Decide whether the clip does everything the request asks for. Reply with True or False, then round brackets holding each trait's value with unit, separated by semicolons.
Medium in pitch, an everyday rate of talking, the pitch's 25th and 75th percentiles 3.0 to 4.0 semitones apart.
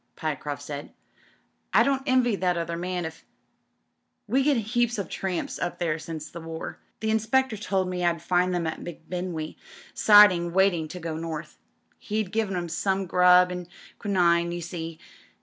True (180 Hz; 170 wpm; 3.4 semitones)